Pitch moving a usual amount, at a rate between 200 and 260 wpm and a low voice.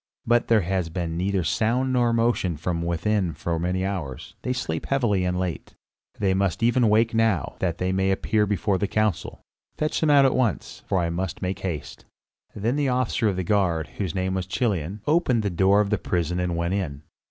Yes: average, 4.3 semitones; fast, 205 wpm; very low, 95 Hz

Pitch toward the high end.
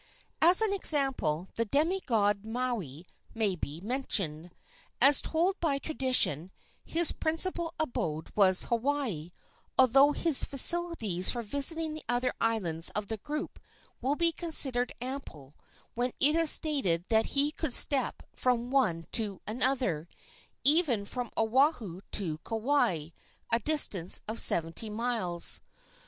Yes: high, 245 Hz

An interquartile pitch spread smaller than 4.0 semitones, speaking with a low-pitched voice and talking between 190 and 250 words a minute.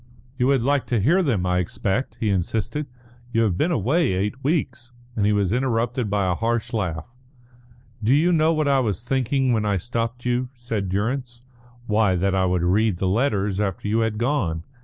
No: average, 4.6 semitones; low, 115 Hz; average, 195 wpm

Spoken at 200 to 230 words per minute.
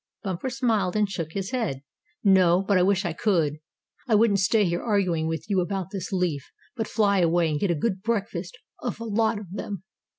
Yes: fast, 205 wpm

